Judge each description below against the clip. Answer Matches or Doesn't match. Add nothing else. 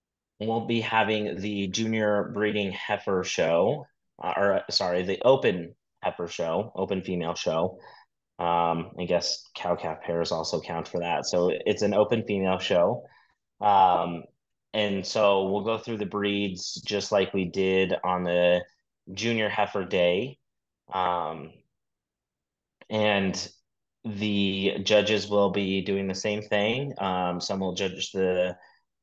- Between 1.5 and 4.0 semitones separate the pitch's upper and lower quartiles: Matches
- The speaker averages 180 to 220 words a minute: Doesn't match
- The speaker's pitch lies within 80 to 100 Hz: Matches